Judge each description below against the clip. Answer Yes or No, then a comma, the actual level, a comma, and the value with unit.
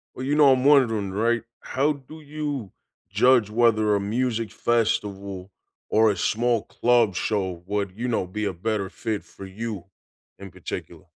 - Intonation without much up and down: No, average, 3.6 semitones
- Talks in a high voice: No, low, 110 Hz